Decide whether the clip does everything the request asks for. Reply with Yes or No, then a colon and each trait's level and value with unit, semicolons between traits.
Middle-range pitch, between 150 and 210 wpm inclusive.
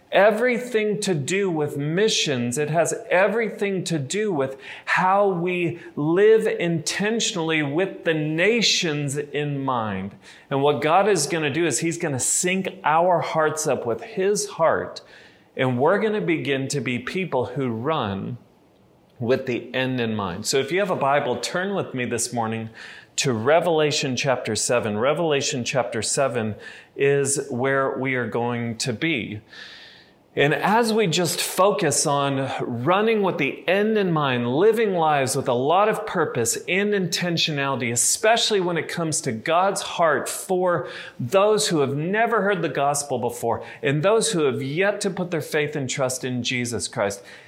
Yes: medium, 155 Hz; average, 165 wpm